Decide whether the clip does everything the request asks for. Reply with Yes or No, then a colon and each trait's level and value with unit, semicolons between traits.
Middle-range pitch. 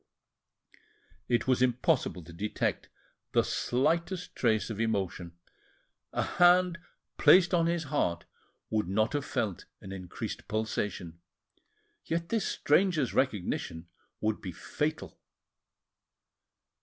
No: low, 120 Hz